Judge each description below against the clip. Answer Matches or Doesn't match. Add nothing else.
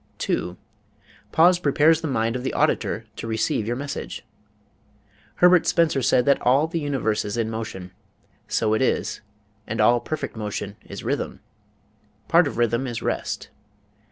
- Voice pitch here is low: Matches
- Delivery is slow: Doesn't match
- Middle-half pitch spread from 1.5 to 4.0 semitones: Doesn't match